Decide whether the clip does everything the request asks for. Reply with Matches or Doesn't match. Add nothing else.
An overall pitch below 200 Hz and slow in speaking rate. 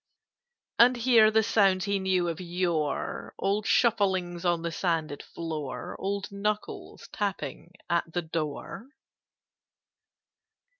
Matches